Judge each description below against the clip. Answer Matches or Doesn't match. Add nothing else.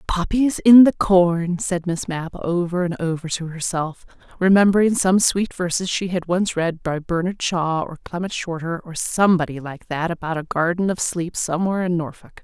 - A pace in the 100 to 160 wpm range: Doesn't match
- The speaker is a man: Doesn't match